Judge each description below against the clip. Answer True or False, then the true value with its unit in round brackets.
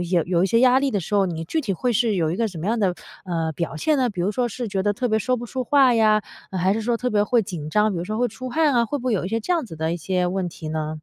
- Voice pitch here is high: True (210 Hz)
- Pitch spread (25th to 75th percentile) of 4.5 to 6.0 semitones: True (5.5 semitones)